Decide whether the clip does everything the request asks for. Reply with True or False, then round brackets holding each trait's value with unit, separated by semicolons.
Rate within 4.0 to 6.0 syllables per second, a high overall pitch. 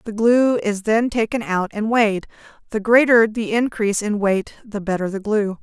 True (4.9 syllables/s; 215 Hz)